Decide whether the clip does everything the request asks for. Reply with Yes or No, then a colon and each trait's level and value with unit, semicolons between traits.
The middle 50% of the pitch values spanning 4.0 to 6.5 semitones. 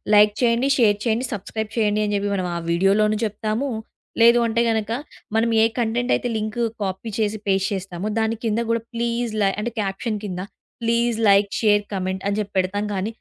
No: narrow, 2.6 semitones